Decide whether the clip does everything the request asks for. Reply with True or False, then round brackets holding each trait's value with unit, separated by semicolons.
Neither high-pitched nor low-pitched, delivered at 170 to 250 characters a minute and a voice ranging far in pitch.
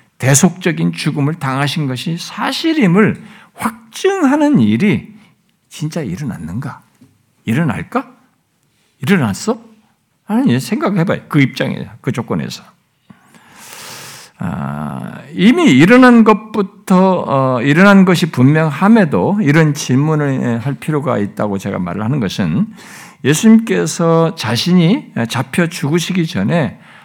True (175 Hz; 245 characters per minute; 6.7 semitones)